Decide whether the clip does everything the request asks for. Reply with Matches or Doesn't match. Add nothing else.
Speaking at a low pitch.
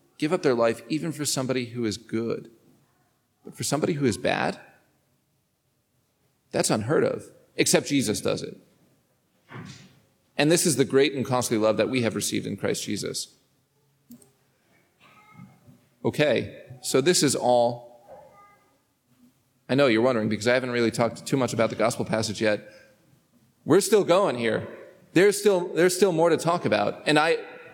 Matches